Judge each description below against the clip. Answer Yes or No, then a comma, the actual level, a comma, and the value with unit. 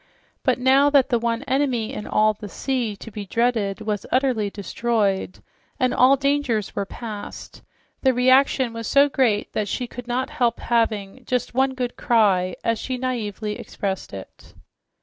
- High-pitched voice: Yes, high, 235 Hz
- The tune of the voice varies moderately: Yes, average, 3.5 semitones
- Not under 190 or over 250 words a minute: No, average, 165 wpm